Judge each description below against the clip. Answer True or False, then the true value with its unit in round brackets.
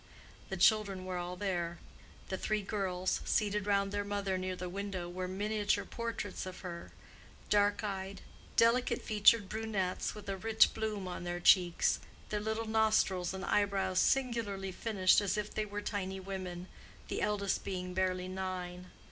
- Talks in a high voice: True (195 Hz)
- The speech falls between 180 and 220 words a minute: False (155 wpm)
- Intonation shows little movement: True (2.2 semitones)